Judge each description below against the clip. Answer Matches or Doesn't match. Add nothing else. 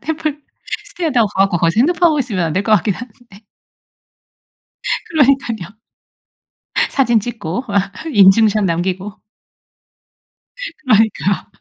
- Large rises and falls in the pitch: Matches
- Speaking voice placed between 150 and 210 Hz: Doesn't match